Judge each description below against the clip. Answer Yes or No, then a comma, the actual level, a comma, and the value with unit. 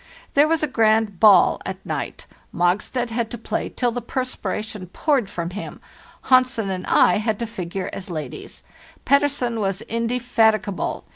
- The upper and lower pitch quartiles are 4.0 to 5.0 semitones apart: Yes, average, 4.3 semitones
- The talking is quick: No, average, 155 wpm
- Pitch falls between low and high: No, high, 220 Hz